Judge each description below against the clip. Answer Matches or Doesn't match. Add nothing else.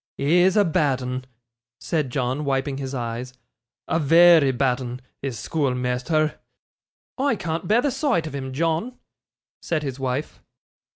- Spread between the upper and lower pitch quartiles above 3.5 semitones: Matches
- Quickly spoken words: Doesn't match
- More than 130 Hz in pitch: Matches